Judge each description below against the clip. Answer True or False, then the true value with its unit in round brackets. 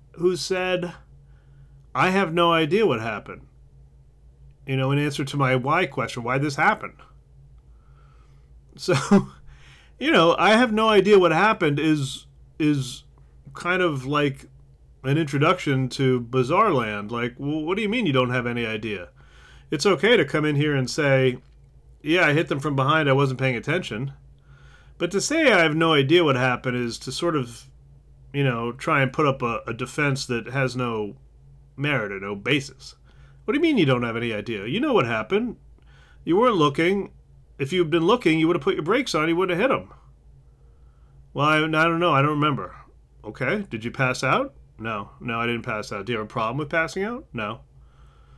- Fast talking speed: False (195 wpm)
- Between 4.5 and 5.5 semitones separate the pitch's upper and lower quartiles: True (5.0 semitones)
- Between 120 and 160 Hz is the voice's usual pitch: True (135 Hz)